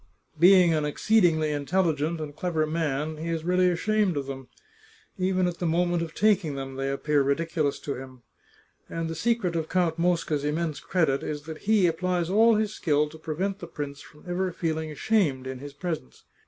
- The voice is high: No, medium, 160 Hz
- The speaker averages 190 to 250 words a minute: Yes, average, 195 wpm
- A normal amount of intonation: Yes, average, 3.5 semitones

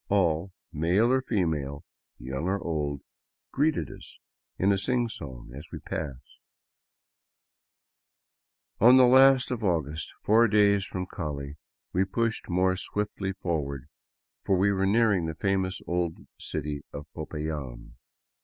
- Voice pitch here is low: Yes, very low, 90 Hz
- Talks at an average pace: No, slow, 130 wpm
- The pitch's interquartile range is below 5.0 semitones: No, wide, 5.5 semitones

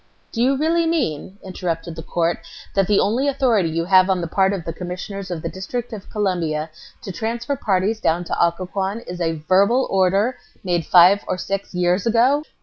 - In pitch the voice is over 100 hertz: Yes, high, 190 Hz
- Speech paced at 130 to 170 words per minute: No, average, 190 wpm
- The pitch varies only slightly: No, average, 4.3 semitones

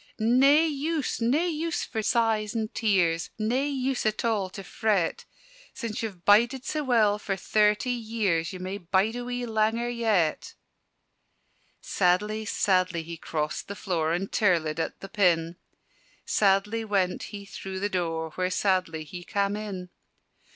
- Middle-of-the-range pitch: No, high, 205 Hz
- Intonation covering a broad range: No, average, 4.1 semitones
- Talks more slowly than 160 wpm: Yes, average, 150 wpm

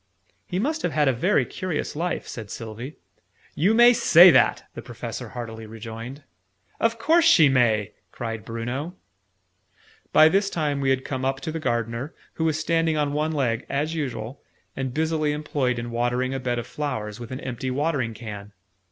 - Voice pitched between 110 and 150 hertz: Yes, low, 135 Hz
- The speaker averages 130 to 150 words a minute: No, average, 180 wpm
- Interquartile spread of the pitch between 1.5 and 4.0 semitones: No, average, 5.2 semitones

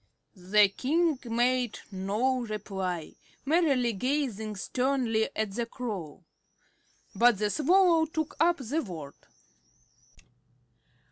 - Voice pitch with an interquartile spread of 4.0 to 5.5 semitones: Yes, average, 5.2 semitones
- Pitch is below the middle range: No, high, 240 Hz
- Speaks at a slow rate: Yes, slow, 95 wpm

